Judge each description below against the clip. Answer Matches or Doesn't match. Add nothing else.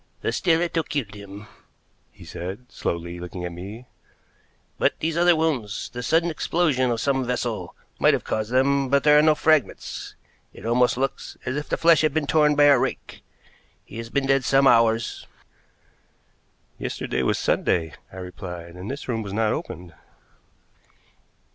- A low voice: Matches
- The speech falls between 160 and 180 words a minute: Matches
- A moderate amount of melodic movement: Doesn't match